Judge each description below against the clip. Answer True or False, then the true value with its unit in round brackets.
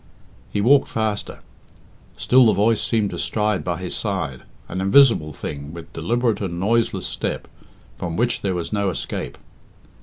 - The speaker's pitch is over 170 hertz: False (100 Hz)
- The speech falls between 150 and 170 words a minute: True (155 wpm)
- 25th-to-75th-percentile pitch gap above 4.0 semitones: True (4.6 semitones)